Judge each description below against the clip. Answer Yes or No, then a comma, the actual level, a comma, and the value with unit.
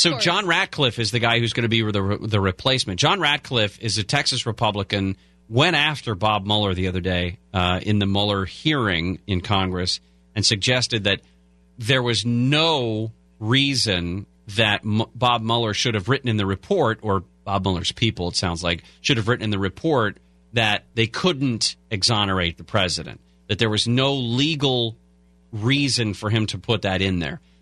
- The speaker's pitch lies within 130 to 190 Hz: No, low, 110 Hz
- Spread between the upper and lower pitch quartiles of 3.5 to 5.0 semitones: Yes, average, 4.4 semitones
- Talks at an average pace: Yes, average, 180 wpm